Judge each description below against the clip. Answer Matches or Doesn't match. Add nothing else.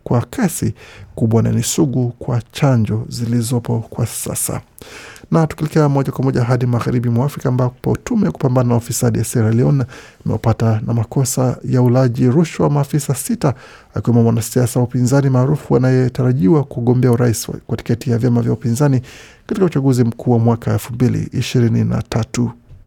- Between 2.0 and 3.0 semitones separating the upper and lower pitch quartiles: Matches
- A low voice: Matches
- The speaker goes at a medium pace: Doesn't match